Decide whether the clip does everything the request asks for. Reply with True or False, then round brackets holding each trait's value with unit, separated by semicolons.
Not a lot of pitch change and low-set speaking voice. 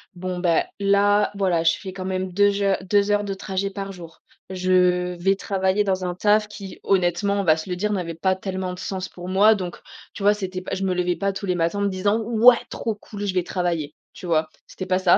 False (1.9 semitones; 190 Hz)